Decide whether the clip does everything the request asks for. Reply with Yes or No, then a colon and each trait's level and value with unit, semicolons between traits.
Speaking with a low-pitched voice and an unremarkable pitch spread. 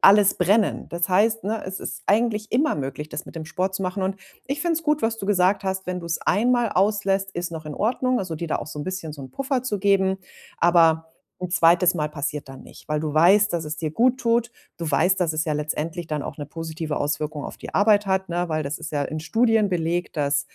No: medium, 180 Hz; average, 4.7 semitones